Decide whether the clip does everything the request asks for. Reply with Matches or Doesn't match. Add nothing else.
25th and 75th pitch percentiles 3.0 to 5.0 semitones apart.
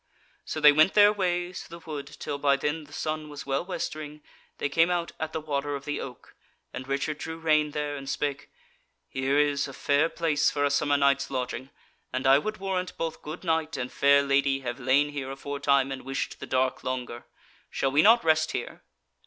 Doesn't match